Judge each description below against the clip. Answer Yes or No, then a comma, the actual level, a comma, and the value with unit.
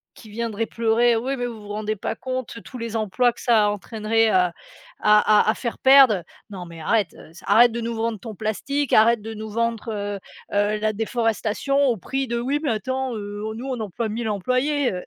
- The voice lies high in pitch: Yes, high, 225 Hz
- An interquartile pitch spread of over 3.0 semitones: No, narrow, 2.4 semitones